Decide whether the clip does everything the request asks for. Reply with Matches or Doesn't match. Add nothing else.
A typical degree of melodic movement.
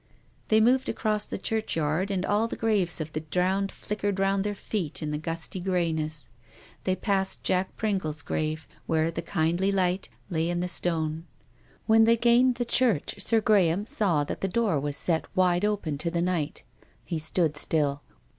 Matches